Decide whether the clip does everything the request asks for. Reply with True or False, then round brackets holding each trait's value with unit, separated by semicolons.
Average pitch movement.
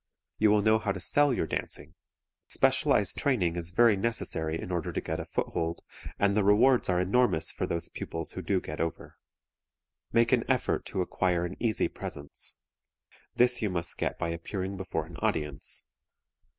True (4.6 semitones)